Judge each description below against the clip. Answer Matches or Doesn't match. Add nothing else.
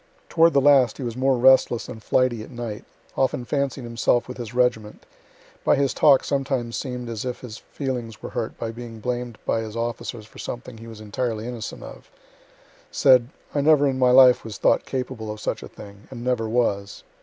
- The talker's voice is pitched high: Doesn't match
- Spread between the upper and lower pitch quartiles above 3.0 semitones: Doesn't match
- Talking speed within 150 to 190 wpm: Doesn't match